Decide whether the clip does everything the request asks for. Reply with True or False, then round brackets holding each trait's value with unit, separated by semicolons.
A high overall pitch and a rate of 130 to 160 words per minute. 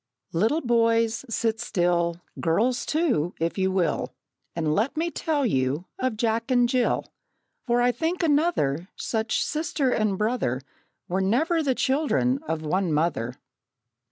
True (225 Hz; 140 wpm)